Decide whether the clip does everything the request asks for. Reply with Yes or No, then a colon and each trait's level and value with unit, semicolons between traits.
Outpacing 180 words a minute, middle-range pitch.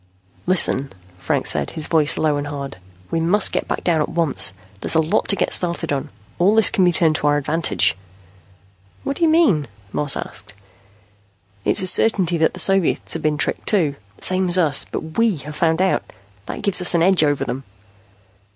Yes: average, 200 wpm; medium, 165 Hz